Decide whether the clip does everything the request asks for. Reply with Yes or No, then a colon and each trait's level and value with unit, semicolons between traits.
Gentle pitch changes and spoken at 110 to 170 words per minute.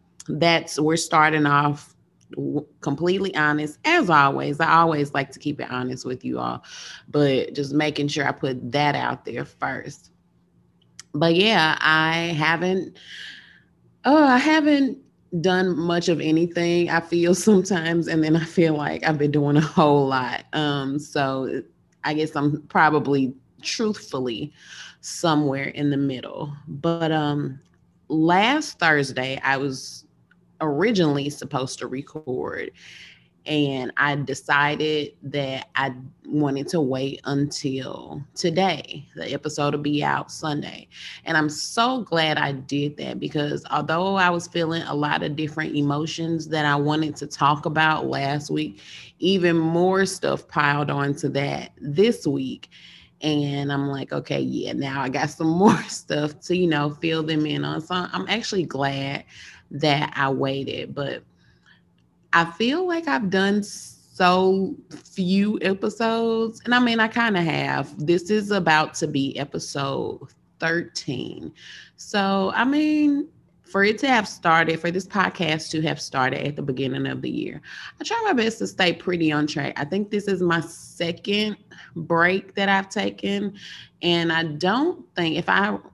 No: average, 4.3 semitones; average, 150 wpm